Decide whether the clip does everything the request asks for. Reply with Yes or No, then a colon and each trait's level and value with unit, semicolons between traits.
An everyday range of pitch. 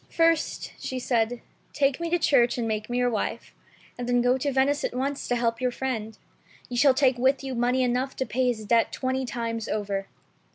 No: narrow, 2.1 semitones